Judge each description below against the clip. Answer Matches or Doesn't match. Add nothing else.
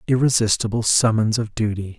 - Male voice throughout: Matches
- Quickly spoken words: Doesn't match